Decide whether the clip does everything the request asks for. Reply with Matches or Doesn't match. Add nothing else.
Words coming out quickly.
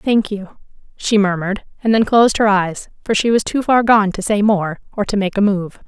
Matches